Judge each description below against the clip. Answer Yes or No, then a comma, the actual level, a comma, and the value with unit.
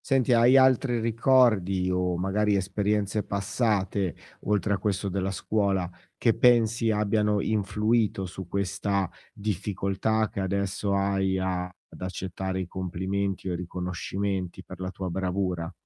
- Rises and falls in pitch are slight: Yes, narrow, 2.2 semitones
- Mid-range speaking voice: No, low, 100 Hz